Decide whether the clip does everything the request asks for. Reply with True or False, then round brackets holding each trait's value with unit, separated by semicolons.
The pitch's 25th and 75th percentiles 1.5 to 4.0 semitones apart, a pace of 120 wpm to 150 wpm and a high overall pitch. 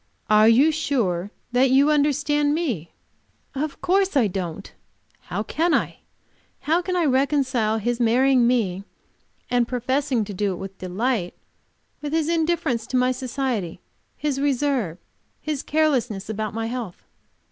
False (5.2 semitones; 140 wpm; 255 Hz)